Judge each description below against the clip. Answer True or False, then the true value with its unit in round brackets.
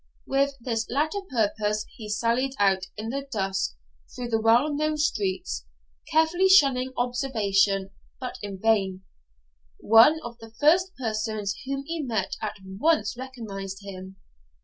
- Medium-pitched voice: False (225 Hz)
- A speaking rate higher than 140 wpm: False (135 wpm)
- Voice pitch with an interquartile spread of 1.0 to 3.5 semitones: False (5.2 semitones)